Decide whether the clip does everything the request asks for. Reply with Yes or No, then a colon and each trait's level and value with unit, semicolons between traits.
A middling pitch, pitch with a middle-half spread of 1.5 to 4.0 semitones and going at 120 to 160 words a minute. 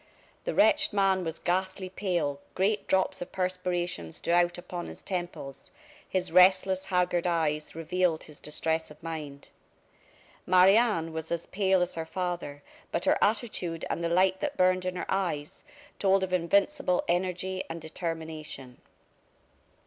Yes: medium, 180 Hz; narrow, 2.5 semitones; average, 150 wpm